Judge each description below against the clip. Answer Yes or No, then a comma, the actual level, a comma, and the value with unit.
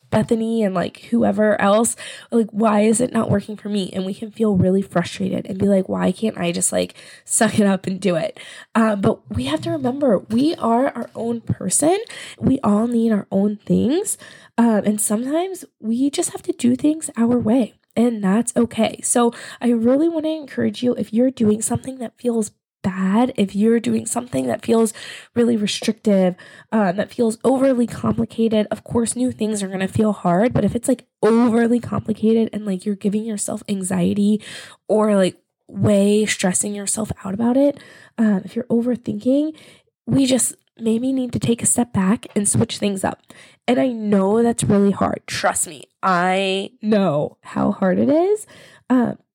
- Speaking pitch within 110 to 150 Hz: No, high, 220 Hz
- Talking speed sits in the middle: Yes, average, 185 wpm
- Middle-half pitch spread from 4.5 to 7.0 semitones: No, average, 3.1 semitones